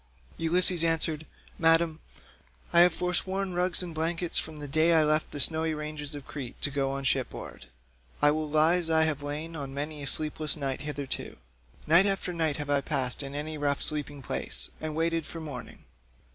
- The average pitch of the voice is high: No, medium, 155 Hz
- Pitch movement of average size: No, narrow, 2.3 semitones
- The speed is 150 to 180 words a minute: No, average, 190 wpm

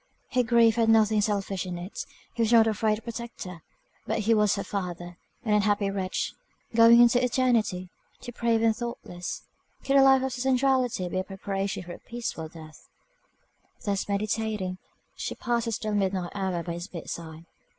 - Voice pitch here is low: No, high, 210 Hz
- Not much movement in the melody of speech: No, average, 4.0 semitones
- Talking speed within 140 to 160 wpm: No, average, 170 wpm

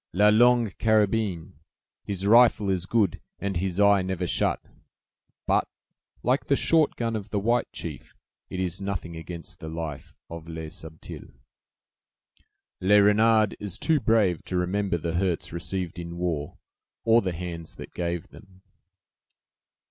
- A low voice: Yes, very low, 95 Hz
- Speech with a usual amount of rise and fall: Yes, average, 3.9 semitones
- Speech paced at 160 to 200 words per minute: No, average, 145 wpm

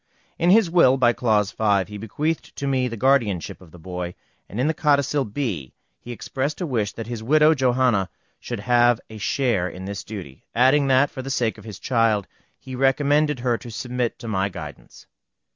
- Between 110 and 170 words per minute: No, average, 195 wpm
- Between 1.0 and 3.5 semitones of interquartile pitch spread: No, average, 4.7 semitones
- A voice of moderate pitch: No, low, 120 Hz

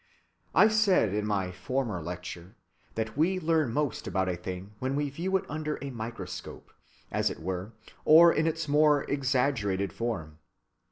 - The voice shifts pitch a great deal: Yes, wide, 8.1 semitones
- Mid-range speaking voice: No, low, 125 Hz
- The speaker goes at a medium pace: Yes, average, 160 wpm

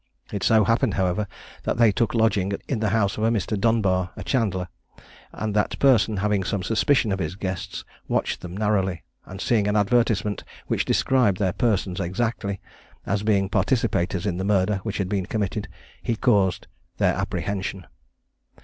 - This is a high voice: No, low, 100 Hz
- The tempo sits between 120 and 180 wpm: Yes, average, 165 wpm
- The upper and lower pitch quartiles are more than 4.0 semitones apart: No, average, 2.7 semitones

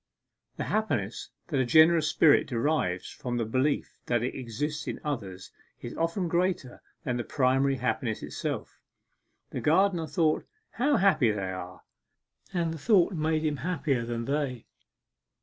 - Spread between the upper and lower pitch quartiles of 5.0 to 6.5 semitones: Yes, wide, 5.4 semitones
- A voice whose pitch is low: No, medium, 145 Hz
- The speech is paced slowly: No, average, 150 wpm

